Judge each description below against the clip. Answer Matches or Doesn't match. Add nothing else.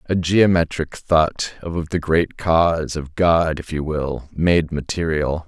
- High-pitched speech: Doesn't match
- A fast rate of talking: Doesn't match